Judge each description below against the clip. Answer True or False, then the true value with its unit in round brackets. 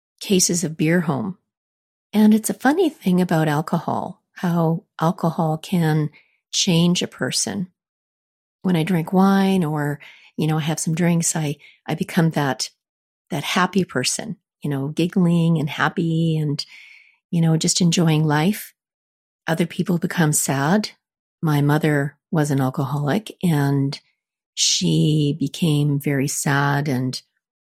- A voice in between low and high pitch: True (165 Hz)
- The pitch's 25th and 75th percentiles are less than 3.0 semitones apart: False (3.7 semitones)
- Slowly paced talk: True (130 wpm)